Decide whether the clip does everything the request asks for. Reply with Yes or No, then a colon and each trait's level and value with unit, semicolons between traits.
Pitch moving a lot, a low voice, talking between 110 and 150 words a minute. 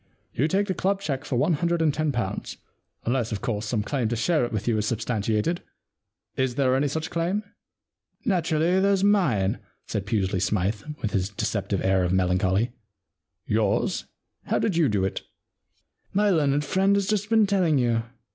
No: wide, 8.5 semitones; low, 130 Hz; average, 185 wpm